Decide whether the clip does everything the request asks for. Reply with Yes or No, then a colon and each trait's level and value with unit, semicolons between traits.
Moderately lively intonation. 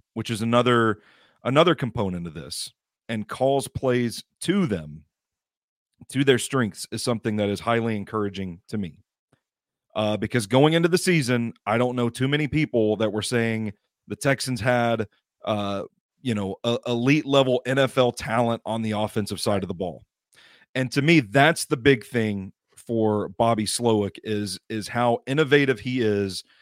Yes: average, 3.5 semitones